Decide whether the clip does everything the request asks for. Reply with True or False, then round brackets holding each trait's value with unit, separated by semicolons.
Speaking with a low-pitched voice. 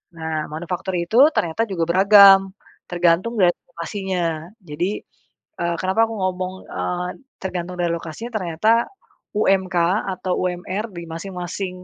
False (180 Hz)